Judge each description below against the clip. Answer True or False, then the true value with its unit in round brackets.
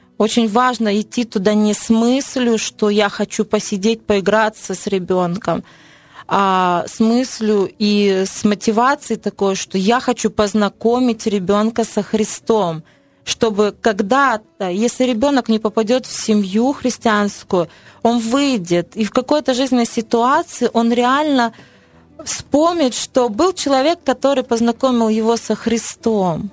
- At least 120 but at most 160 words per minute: True (125 wpm)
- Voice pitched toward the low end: False (225 Hz)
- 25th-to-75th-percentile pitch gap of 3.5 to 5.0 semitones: False (3.1 semitones)